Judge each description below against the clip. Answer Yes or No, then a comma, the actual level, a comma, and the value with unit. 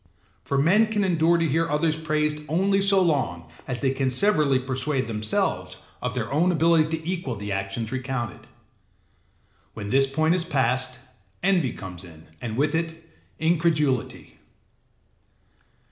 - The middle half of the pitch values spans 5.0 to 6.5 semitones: No, average, 4.5 semitones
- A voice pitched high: No, medium, 150 Hz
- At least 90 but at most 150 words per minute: Yes, average, 145 wpm